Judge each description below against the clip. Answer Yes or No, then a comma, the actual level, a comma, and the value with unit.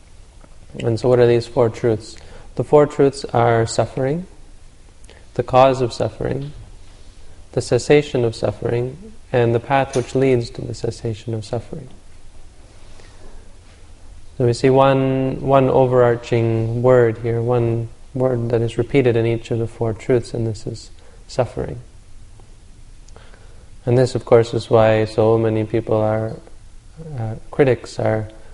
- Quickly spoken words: No, average, 140 wpm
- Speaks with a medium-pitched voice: No, low, 115 Hz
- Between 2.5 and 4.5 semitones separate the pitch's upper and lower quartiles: Yes, average, 3.3 semitones